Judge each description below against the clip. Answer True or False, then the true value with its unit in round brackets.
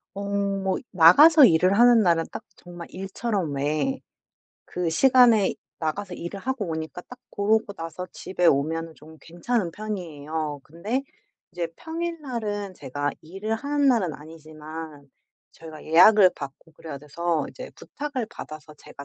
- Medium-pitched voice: True (180 Hz)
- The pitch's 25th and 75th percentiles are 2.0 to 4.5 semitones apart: False (5.5 semitones)